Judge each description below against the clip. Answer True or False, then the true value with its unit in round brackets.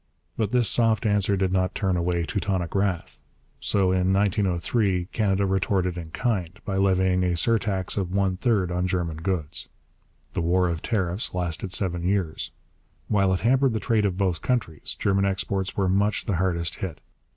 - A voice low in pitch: True (95 Hz)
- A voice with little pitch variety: True (2.1 semitones)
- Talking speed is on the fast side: False (170 wpm)